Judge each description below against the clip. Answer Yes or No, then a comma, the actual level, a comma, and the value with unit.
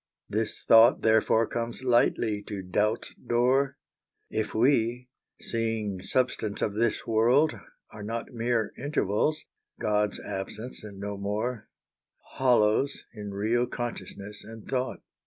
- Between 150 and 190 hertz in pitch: No, low, 115 Hz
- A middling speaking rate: No, slow, 120 wpm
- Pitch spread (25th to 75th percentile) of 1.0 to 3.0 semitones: Yes, narrow, 2.6 semitones